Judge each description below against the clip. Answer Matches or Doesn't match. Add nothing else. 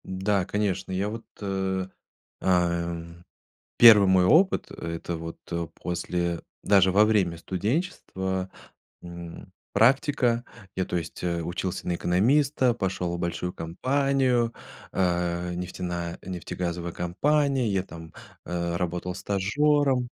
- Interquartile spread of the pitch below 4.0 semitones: Doesn't match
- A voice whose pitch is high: Doesn't match